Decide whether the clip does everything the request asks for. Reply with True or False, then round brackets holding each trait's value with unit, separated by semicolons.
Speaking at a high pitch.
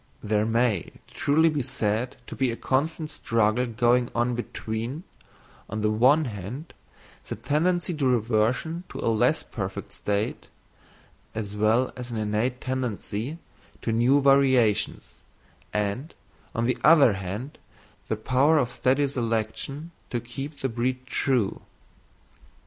False (125 Hz)